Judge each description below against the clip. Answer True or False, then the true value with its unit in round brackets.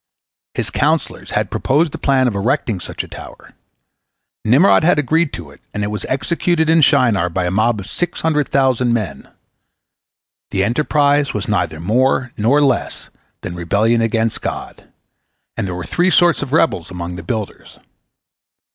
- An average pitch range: False (6.9 semitones)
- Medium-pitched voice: False (120 Hz)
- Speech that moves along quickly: False (165 wpm)